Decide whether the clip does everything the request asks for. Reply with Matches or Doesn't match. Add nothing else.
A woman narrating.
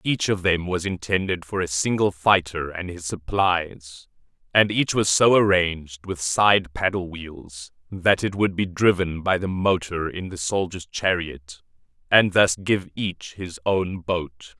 Doesn't match